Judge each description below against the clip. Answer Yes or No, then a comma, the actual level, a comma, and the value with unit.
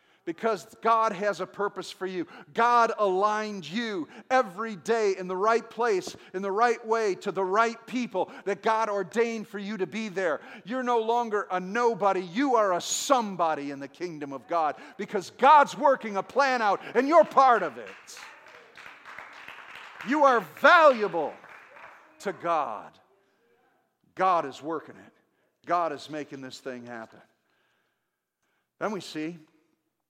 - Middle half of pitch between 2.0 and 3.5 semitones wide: No, average, 4.2 semitones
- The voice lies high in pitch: Yes, high, 210 Hz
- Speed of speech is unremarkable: Yes, average, 150 wpm